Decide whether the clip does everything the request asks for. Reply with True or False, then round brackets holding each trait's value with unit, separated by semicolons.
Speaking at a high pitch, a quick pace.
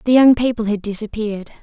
False (220 Hz; 185 wpm)